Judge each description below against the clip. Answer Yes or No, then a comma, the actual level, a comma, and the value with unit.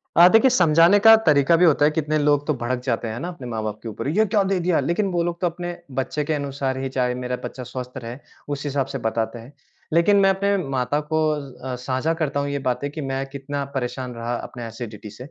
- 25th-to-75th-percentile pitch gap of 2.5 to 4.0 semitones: No, average, 4.9 semitones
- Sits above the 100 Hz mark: Yes, medium, 140 Hz